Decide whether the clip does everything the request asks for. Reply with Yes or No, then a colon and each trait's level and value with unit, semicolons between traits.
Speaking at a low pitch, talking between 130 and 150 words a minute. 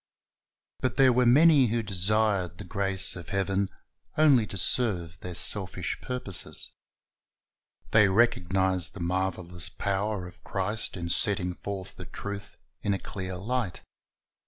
Yes: very low, 95 Hz; slow, 135 wpm